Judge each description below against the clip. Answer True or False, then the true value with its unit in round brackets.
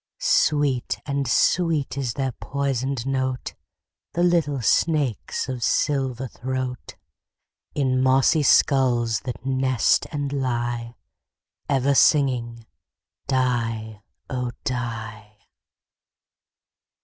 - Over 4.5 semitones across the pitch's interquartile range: False (2.6 semitones)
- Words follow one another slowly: True (90 wpm)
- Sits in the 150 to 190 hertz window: False (130 Hz)